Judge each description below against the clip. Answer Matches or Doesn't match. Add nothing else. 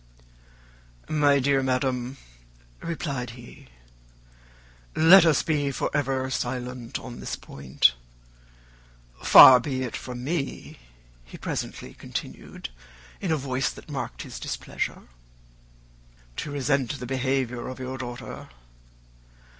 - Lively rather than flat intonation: Doesn't match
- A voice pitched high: Doesn't match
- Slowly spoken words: Matches